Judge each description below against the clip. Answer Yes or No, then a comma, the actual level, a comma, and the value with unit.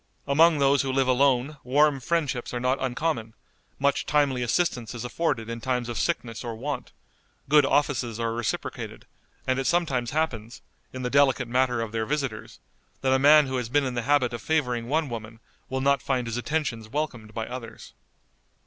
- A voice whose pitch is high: No, low, 130 Hz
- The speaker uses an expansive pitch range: No, average, 3.2 semitones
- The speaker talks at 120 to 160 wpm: No, average, 185 wpm